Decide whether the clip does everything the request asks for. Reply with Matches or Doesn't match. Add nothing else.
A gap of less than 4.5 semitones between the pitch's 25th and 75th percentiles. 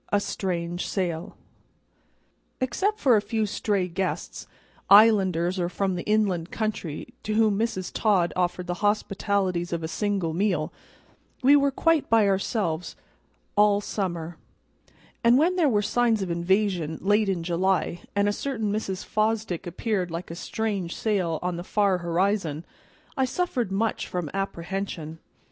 Matches